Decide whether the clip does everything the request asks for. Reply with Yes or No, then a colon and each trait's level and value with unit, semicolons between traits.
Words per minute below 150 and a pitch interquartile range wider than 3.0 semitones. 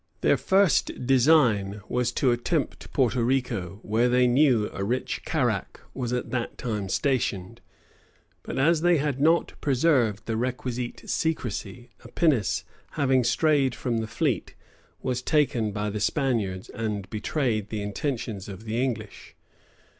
Yes: average, 140 wpm; average, 3.9 semitones